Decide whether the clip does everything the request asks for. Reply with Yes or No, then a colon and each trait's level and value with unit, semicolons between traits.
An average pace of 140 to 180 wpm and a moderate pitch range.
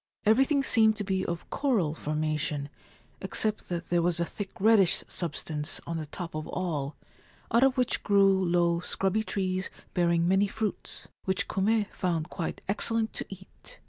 Yes: average, 160 wpm; average, 4.0 semitones